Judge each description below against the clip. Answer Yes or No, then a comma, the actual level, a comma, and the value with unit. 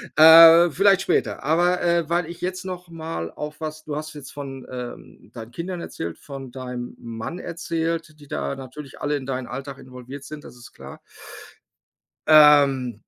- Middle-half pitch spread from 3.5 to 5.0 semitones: Yes, average, 4.4 semitones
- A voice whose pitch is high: No, medium, 150 Hz